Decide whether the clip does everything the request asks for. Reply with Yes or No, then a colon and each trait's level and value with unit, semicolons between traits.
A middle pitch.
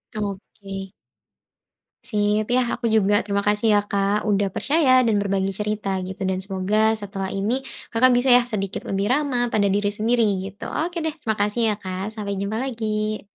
No: high, 210 Hz